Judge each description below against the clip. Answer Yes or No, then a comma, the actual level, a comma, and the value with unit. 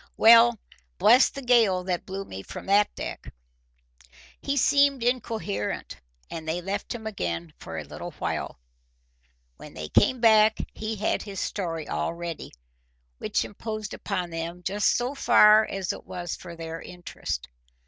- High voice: Yes, high, 200 Hz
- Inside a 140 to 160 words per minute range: Yes, average, 150 wpm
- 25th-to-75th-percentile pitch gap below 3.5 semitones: No, average, 4.6 semitones